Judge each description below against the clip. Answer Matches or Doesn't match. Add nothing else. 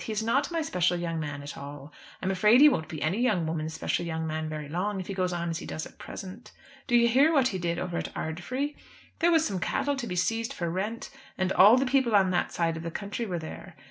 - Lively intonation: Matches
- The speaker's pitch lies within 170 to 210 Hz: Matches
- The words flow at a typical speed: Doesn't match